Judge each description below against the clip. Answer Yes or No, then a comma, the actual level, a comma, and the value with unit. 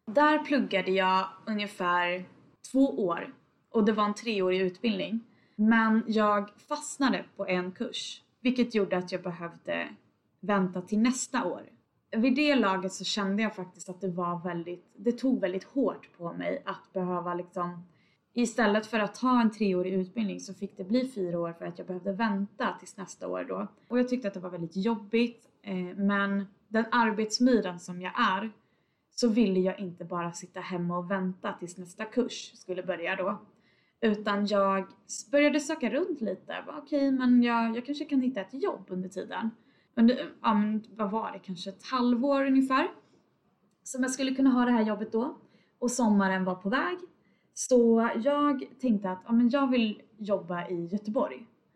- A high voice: Yes, high, 210 Hz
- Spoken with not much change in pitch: No, average, 4.4 semitones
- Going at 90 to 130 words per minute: No, average, 175 wpm